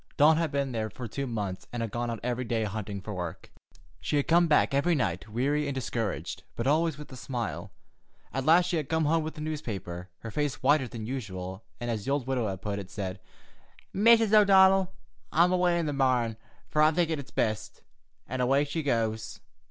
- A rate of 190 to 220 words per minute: Yes, fast, 205 wpm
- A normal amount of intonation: No, wide, 5.9 semitones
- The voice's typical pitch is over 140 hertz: No, low, 130 Hz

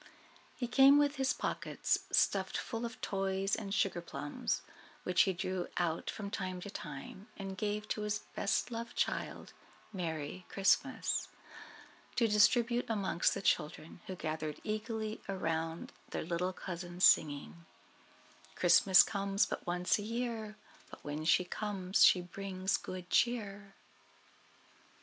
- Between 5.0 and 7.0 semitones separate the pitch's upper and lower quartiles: No, average, 3.3 semitones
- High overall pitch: Yes, high, 195 Hz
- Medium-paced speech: No, slow, 130 wpm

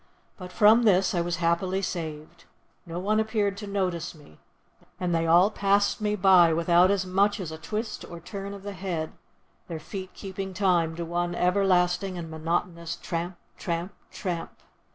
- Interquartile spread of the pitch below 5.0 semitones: Yes, average, 2.7 semitones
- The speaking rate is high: No, average, 170 wpm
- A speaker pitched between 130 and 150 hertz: No, medium, 180 Hz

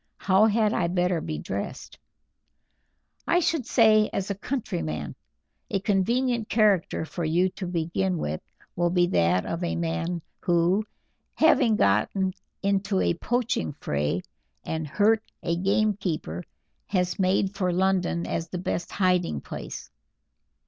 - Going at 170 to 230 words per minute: No, slow, 135 wpm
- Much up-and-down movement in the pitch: No, average, 3.6 semitones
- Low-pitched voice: No, medium, 185 Hz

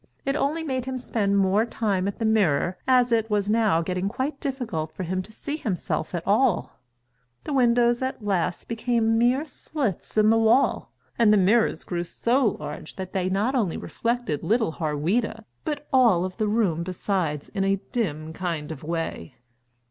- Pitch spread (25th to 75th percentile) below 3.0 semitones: No, average, 4.9 semitones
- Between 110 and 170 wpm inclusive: No, average, 180 wpm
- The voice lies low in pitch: No, high, 210 Hz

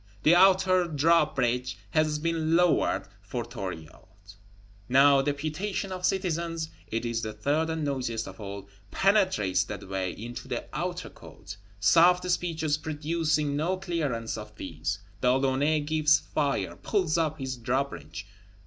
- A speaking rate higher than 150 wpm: No, slow, 135 wpm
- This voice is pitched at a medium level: Yes, medium, 145 Hz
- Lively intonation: Yes, wide, 6.3 semitones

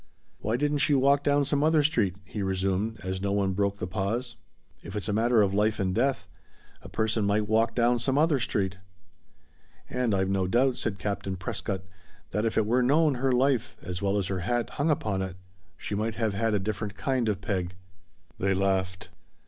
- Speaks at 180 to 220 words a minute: Yes, average, 200 wpm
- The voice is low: Yes, low, 105 Hz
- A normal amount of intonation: Yes, average, 4.3 semitones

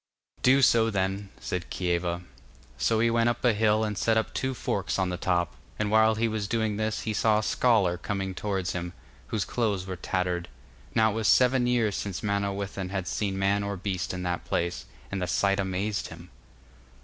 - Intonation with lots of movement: No, average, 3.0 semitones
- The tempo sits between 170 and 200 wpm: Yes, average, 195 wpm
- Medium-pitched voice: No, low, 100 Hz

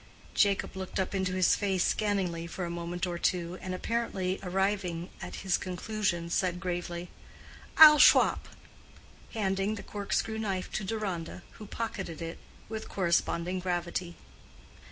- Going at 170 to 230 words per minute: No, average, 140 wpm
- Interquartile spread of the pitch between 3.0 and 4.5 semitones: No, narrow, 2.5 semitones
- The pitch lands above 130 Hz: Yes, medium, 185 Hz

